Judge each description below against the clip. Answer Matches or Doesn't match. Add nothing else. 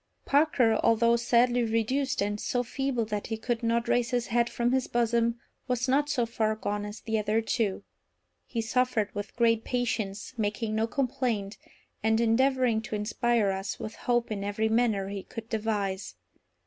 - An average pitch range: Doesn't match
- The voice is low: Doesn't match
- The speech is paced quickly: Doesn't match